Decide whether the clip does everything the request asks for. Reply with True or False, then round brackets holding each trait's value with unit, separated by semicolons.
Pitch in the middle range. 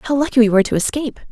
False (250 Hz)